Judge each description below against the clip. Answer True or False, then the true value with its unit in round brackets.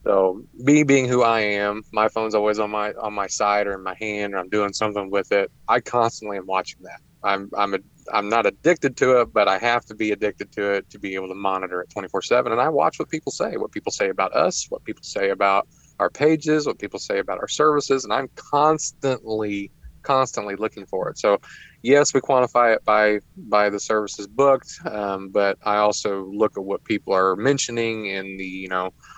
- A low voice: True (105 Hz)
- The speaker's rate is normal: False (220 wpm)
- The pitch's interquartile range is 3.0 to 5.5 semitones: True (3.8 semitones)